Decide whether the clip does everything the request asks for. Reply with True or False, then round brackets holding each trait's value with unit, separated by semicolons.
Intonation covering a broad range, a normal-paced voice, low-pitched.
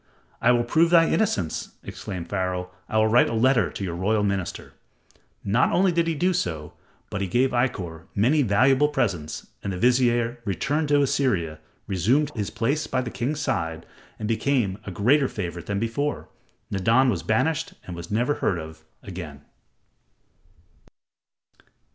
True (6.5 semitones; 160 wpm; 115 Hz)